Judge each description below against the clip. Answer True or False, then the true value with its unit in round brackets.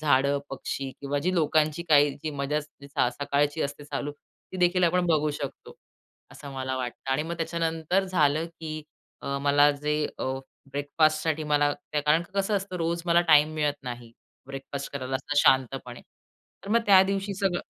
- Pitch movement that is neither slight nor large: True (3.1 semitones)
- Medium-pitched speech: True (150 Hz)